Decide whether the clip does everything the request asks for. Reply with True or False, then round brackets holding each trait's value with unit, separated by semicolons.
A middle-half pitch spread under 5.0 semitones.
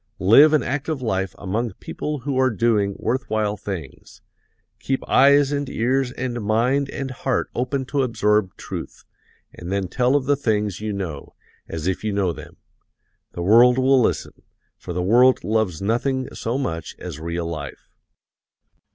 False (5.3 semitones)